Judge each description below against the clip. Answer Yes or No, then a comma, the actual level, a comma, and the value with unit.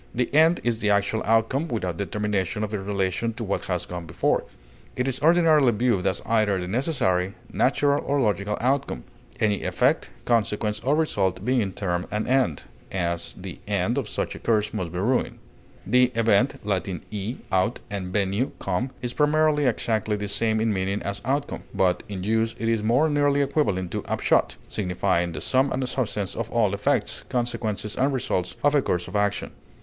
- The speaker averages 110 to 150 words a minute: No, average, 180 wpm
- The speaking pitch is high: No, low, 110 Hz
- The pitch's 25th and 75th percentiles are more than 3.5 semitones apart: Yes, average, 4.7 semitones